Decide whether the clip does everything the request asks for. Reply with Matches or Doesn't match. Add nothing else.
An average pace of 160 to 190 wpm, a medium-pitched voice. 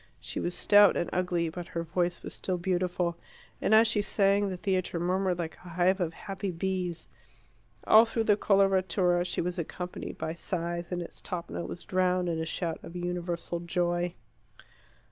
Matches